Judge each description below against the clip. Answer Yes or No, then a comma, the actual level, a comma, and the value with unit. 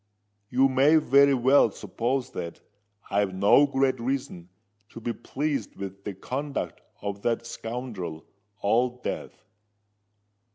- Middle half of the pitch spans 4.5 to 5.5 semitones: Yes, average, 5.0 semitones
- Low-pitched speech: Yes, low, 125 Hz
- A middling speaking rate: No, slow, 120 wpm